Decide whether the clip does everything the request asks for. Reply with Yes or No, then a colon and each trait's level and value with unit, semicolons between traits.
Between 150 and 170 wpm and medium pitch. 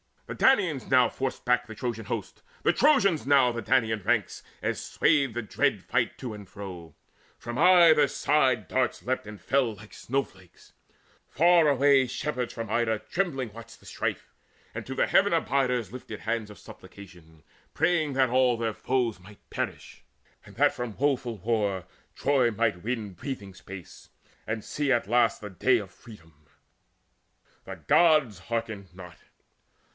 No: average, 160 wpm; low, 120 Hz